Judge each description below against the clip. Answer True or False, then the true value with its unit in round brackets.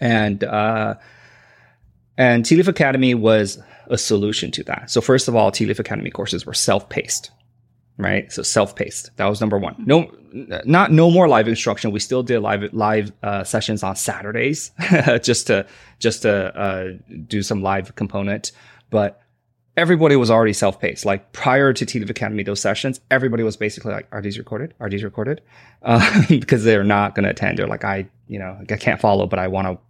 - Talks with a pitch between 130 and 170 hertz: False (110 Hz)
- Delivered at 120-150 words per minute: False (185 wpm)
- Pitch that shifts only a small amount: False (3.4 semitones)